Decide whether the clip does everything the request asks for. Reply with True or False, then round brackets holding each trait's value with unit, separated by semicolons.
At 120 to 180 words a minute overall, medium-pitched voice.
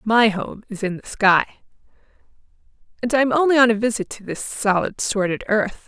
False (175 wpm; 220 Hz)